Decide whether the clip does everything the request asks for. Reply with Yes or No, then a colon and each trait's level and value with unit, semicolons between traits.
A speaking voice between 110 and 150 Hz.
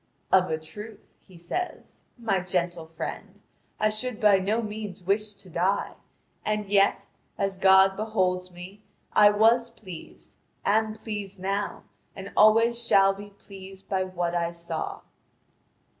No: high, 195 Hz